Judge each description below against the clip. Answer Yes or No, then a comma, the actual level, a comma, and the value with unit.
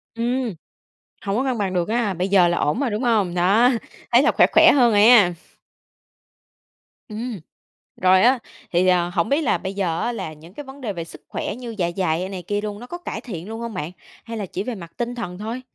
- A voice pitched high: Yes, high, 205 Hz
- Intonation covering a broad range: No, average, 4.9 semitones